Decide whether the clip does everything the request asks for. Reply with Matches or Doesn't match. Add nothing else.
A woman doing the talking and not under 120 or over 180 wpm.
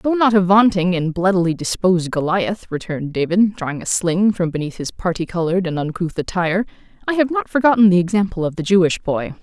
Doesn't match